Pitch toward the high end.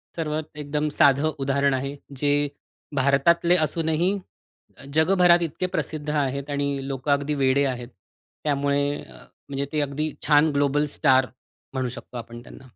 No: medium, 145 Hz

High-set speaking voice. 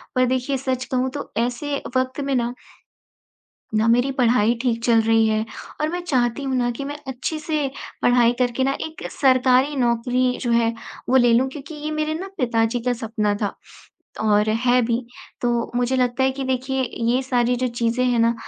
Yes: very high, 250 Hz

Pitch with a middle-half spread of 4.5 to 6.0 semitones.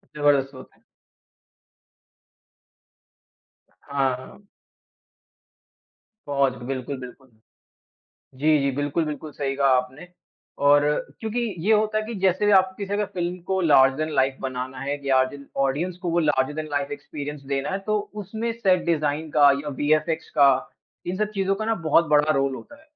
Yes: average, 5.2 semitones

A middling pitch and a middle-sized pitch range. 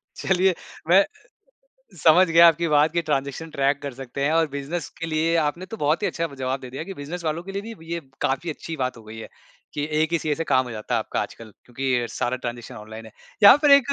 Yes: medium, 150 Hz; average, 4.5 semitones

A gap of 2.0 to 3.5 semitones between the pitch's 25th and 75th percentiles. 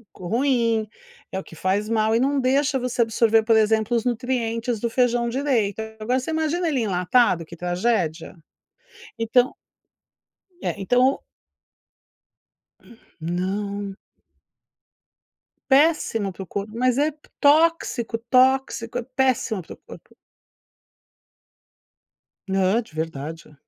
No: average, 4.3 semitones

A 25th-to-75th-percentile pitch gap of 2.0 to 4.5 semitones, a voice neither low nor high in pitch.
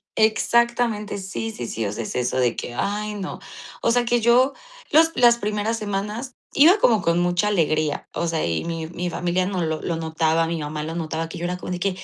No: wide, 5.4 semitones; medium, 180 Hz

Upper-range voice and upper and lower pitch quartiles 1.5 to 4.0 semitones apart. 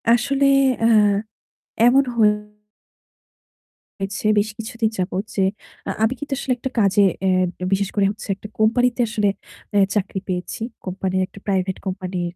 Yes: high, 205 Hz; average, 2.9 semitones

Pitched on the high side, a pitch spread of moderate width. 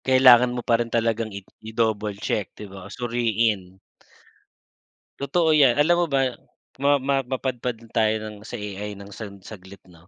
No: low, 115 Hz; average, 3.8 semitones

